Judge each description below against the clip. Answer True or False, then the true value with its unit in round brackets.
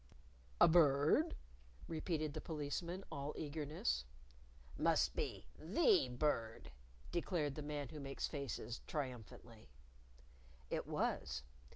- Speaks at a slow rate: True (100 wpm)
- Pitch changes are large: False (3.8 semitones)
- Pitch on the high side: False (145 Hz)